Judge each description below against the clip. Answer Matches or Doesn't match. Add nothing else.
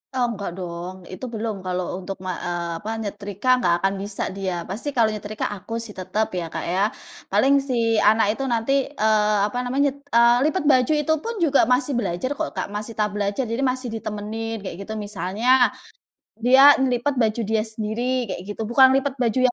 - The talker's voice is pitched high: Matches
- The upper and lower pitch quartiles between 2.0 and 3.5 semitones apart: Doesn't match